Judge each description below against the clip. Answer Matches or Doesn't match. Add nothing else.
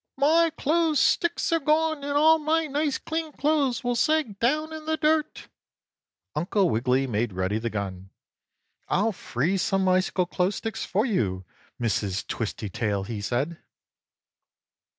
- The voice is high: Matches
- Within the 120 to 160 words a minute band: Matches